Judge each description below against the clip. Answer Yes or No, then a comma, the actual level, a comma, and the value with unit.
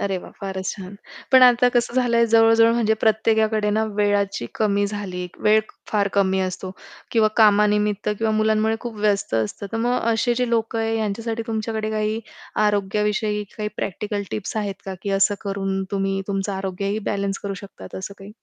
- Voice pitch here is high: Yes, high, 210 Hz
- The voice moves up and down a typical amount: No, narrow, 2.0 semitones